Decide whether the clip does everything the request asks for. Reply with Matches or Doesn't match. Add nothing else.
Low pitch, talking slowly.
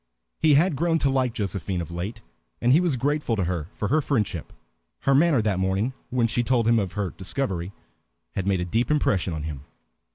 Doesn't match